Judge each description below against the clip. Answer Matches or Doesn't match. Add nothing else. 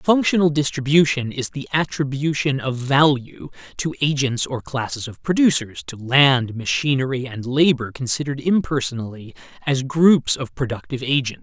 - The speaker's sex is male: Matches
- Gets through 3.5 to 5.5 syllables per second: Matches